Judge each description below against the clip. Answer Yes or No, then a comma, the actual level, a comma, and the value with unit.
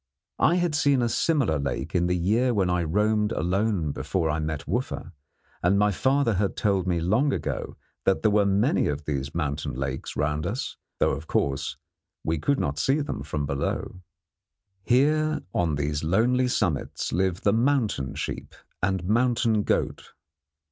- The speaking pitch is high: No, very low, 95 Hz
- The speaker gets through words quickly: No, average, 165 wpm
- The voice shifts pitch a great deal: Yes, wide, 7.5 semitones